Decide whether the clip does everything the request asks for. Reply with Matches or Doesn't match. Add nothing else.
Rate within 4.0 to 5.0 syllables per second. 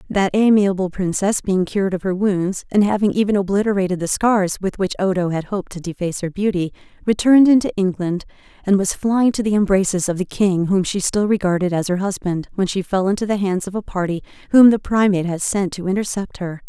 Doesn't match